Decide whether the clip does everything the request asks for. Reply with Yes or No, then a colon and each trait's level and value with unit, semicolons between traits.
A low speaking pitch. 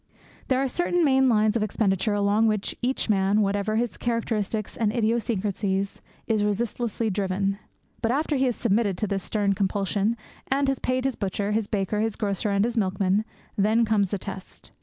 No: high, 215 Hz